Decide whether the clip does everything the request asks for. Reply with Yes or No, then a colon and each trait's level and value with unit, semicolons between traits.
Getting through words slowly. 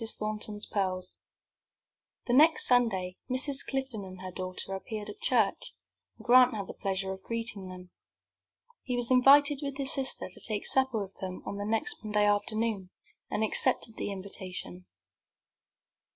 No: average, 150 wpm